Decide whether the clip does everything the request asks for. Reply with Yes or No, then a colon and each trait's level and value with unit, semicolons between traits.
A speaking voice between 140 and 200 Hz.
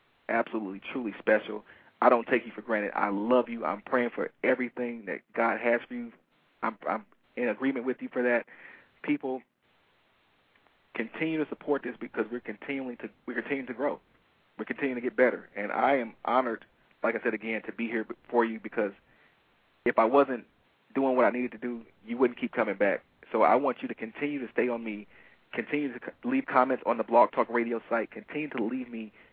No: low, 125 Hz